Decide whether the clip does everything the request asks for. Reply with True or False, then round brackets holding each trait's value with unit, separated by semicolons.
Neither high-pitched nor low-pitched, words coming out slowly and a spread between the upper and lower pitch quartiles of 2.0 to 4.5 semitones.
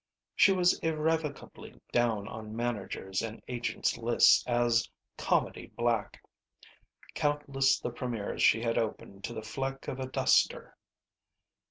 False (120 Hz; 125 wpm; 3.2 semitones)